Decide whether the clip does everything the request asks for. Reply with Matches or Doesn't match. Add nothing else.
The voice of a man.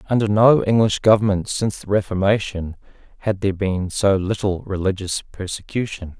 Matches